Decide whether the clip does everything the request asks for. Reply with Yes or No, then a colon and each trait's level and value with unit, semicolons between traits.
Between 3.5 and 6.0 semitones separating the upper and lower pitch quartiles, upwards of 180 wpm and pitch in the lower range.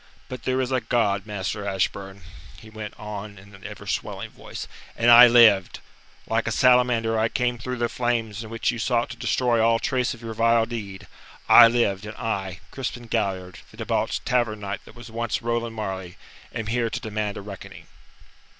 No: average, 2.7 semitones; average, 190 wpm; low, 115 Hz